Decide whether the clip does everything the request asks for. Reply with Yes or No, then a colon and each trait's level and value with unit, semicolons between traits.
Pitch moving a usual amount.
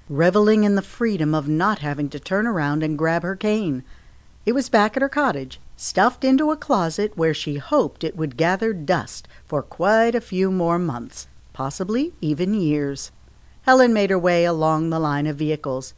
No: wide, 5.8 semitones